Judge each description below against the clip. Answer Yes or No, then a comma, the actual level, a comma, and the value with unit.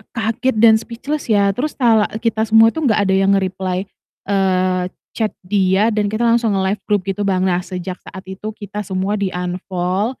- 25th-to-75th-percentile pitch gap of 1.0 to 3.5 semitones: Yes, average, 2.8 semitones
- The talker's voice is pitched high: Yes, high, 200 Hz